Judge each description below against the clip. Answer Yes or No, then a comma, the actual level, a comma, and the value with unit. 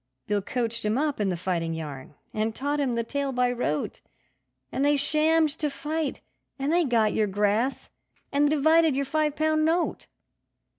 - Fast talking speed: No, average, 170 wpm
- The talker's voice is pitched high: Yes, very high, 270 Hz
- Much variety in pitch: Yes, wide, 6.1 semitones